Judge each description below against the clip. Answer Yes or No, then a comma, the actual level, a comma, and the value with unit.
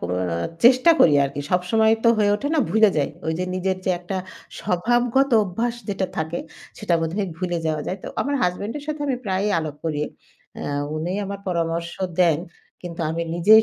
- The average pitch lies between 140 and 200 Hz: Yes, medium, 185 Hz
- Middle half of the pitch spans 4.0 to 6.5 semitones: Yes, average, 4.7 semitones